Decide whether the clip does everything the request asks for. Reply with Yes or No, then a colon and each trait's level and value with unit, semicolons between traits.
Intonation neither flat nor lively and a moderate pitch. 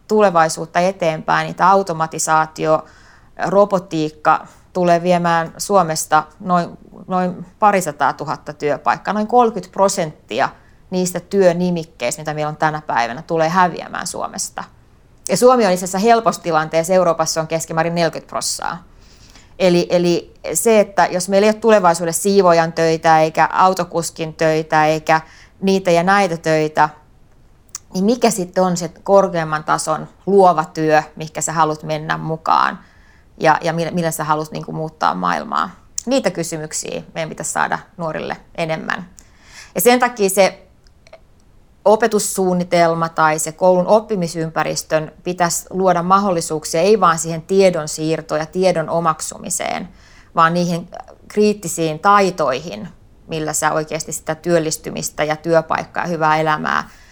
Yes: average, 3.1 semitones; medium, 165 Hz